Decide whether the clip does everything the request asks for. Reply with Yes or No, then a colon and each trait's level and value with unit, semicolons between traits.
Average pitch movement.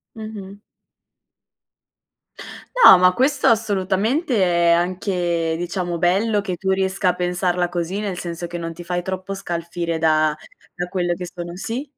No: narrow, 2.2 semitones